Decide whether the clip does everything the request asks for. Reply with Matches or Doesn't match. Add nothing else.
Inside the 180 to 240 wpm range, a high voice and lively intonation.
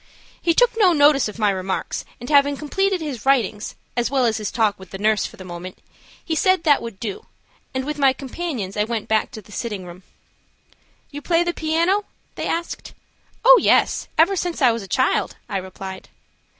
Matches